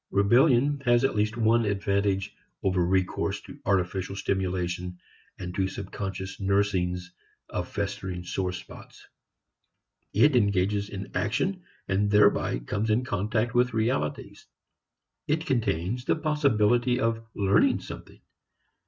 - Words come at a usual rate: No, slow, 120 wpm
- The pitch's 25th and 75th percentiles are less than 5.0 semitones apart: Yes, average, 3.9 semitones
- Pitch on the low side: Yes, low, 100 Hz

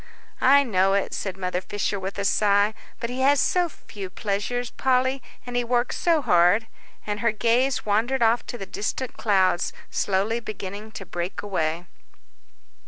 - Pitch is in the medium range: No, high, 210 Hz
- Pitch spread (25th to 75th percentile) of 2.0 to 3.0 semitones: No, average, 4.0 semitones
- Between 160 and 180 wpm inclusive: Yes, average, 165 wpm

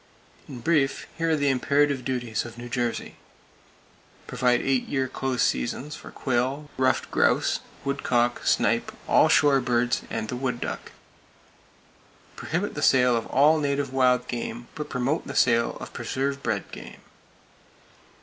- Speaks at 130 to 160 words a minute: Yes, average, 145 wpm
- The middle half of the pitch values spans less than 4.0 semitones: Yes, narrow, 2.5 semitones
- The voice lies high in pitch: No, low, 130 Hz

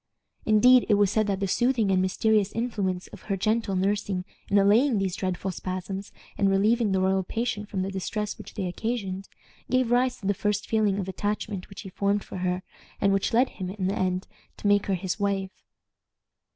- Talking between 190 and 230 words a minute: Yes, average, 200 wpm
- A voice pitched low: No, high, 200 Hz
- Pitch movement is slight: Yes, narrow, 2.1 semitones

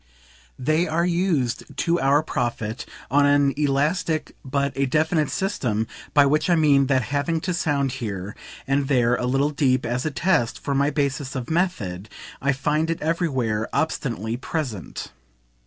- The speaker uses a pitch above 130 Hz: Yes, medium, 140 Hz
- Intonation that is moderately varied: Yes, average, 3.8 semitones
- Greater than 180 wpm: No, average, 155 wpm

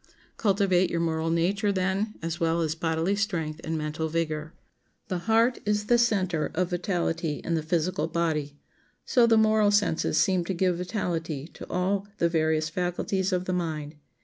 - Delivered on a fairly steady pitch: No, average, 3.4 semitones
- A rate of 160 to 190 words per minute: Yes, average, 170 wpm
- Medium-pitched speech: Yes, medium, 175 Hz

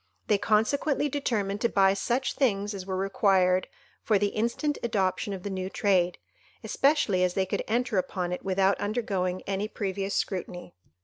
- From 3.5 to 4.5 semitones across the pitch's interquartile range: No, average, 2.8 semitones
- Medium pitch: No, high, 200 Hz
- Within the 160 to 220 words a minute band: Yes, average, 165 wpm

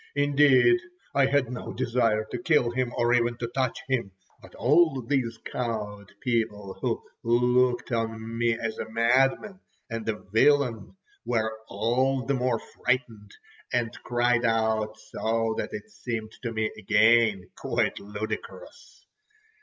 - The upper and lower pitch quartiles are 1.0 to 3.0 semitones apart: Yes, narrow, 2.4 semitones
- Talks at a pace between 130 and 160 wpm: Yes, average, 140 wpm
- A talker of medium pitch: No, low, 115 Hz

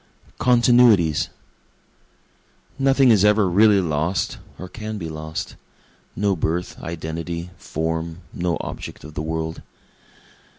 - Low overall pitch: Yes, very low, 85 Hz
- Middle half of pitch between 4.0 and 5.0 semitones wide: Yes, average, 4.6 semitones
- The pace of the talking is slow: Yes, slow, 110 wpm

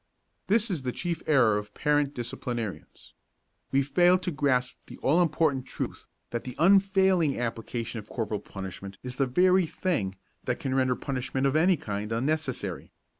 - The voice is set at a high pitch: No, low, 135 Hz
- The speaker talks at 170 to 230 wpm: No, average, 160 wpm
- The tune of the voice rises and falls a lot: Yes, wide, 6.0 semitones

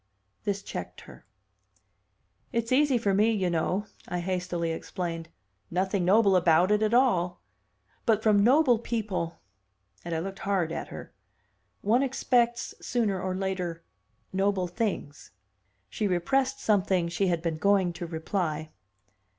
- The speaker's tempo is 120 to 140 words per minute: Yes, slow, 135 wpm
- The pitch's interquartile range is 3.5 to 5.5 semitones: Yes, average, 4.0 semitones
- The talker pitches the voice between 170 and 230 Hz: Yes, high, 190 Hz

